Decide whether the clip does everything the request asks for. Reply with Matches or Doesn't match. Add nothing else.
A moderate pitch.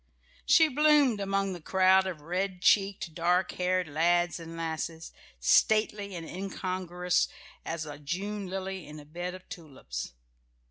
Matches